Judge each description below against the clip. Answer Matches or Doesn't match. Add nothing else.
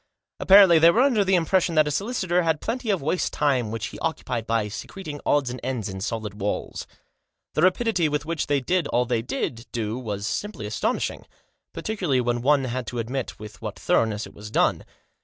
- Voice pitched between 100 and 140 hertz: Matches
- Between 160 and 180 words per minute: Doesn't match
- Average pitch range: Doesn't match